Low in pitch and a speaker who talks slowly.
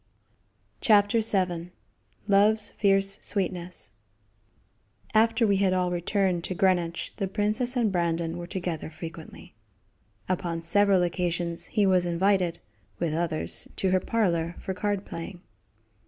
No: medium, 185 Hz; slow, 125 wpm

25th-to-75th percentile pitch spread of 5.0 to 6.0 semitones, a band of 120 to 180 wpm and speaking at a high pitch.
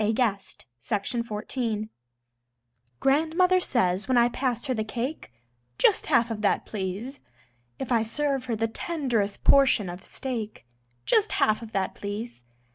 No: average, 3.9 semitones; average, 150 wpm; high, 230 Hz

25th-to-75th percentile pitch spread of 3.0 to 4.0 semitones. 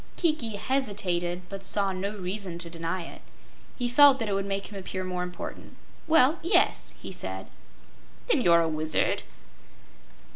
No: average, 5.3 semitones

